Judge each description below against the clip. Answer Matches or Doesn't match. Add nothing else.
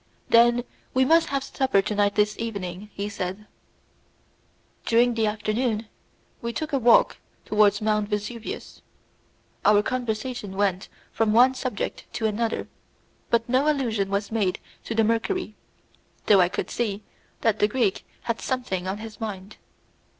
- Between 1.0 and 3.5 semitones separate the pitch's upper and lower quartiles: Matches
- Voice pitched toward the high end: Matches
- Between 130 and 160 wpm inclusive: Matches